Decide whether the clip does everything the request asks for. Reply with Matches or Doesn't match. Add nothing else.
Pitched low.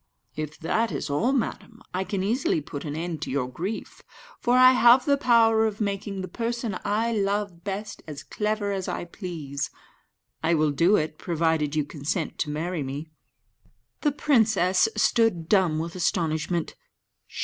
Doesn't match